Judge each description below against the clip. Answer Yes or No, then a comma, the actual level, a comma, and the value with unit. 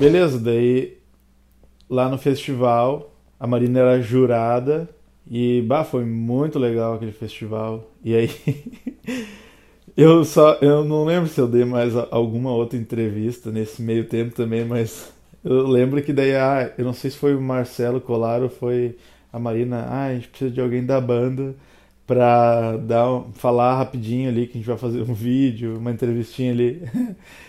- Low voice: Yes, low, 125 Hz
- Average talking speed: Yes, average, 160 wpm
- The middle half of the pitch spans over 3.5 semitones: No, narrow, 2.5 semitones